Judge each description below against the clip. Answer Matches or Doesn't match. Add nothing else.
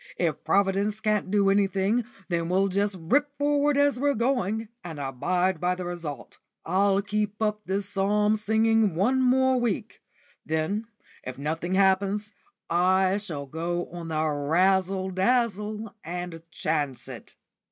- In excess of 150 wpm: Doesn't match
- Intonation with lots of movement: Doesn't match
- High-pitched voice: Matches